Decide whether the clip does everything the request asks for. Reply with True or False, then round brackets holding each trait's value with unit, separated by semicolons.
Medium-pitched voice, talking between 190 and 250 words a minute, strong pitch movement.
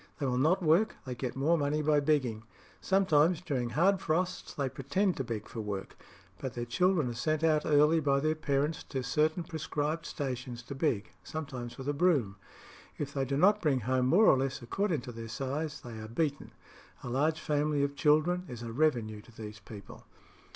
False (145 Hz; 195 wpm; 4.1 semitones)